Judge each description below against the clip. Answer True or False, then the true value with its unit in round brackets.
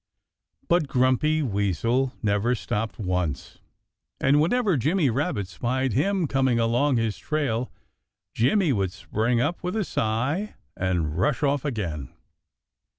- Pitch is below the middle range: True (125 Hz)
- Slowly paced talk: True (125 wpm)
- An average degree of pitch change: False (6.0 semitones)